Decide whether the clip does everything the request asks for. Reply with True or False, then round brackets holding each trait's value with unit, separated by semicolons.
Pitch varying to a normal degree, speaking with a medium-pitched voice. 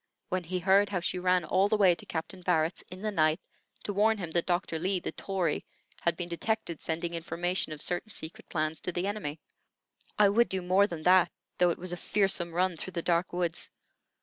False (2.2 semitones; 180 Hz)